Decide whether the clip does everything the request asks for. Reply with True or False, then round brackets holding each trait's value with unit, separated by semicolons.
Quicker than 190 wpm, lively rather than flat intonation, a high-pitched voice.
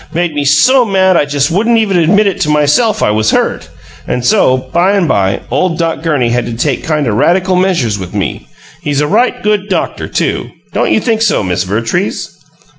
False (200 wpm; 7.5 semitones; 155 Hz)